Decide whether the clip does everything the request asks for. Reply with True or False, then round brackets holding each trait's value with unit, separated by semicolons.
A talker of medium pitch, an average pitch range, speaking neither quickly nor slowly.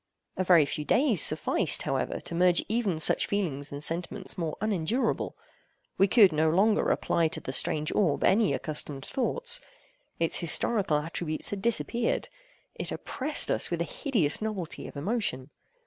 False (180 Hz; 5.7 semitones; 155 wpm)